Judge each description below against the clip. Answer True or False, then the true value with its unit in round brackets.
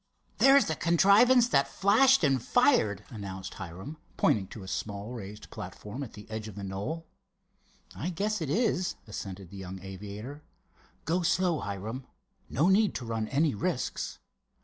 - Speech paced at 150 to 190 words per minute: True (155 wpm)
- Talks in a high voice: False (120 Hz)